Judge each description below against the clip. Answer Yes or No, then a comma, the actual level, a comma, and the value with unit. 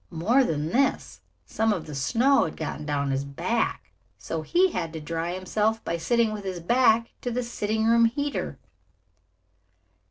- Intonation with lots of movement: Yes, wide, 6.5 semitones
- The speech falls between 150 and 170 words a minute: Yes, average, 165 wpm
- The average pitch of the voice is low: No, high, 210 Hz